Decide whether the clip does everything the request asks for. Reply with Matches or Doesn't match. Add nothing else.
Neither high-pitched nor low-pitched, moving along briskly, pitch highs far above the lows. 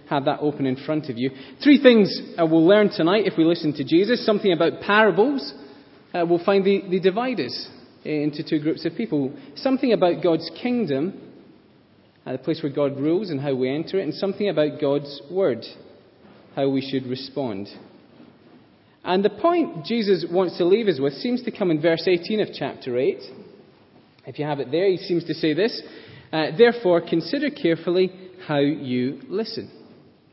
Doesn't match